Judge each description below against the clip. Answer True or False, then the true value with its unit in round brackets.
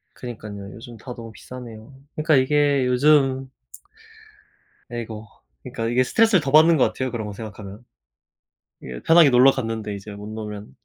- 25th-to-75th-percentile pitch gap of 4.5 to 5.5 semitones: False (4.0 semitones)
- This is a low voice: True (120 Hz)